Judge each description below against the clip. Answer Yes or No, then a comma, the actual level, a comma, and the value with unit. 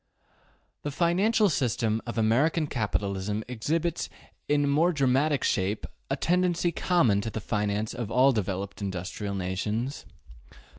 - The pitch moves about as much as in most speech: No, wide, 6.6 semitones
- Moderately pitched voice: No, low, 120 Hz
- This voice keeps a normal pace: No, slow, 120 wpm